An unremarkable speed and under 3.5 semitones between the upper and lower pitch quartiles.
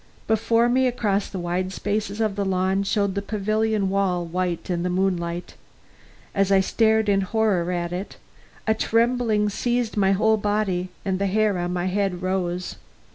Yes: average, 170 wpm; average, 2.9 semitones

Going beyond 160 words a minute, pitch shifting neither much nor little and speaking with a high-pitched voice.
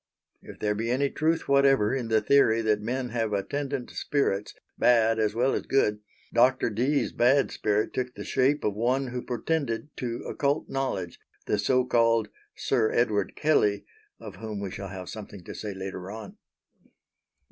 No: average, 170 wpm; average, 4.2 semitones; low, 115 Hz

